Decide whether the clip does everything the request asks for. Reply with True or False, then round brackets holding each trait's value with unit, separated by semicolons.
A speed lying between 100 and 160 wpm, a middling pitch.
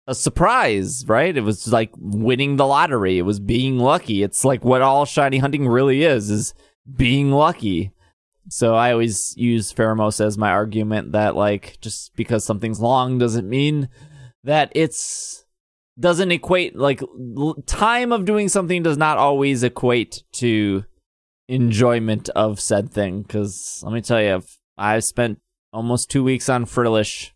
False (155 wpm; 120 Hz)